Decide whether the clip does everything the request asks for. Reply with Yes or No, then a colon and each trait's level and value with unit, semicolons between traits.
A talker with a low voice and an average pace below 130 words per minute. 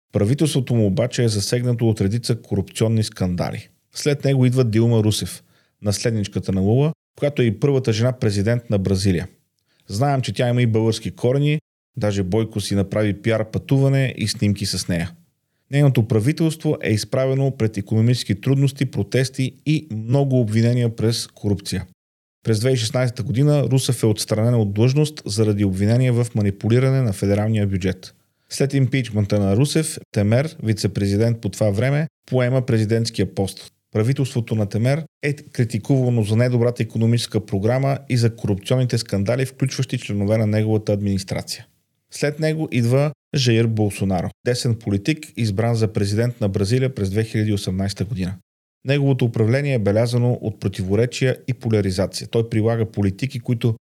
No: low, 115 Hz; average, 140 wpm